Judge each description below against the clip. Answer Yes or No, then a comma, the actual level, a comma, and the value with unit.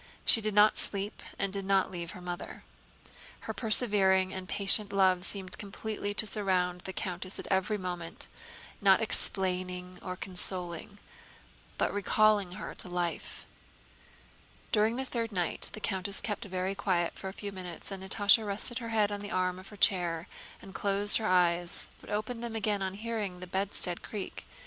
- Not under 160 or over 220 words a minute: Yes, average, 170 wpm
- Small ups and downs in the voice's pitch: Yes, narrow, 2.3 semitones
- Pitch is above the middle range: Yes, high, 195 Hz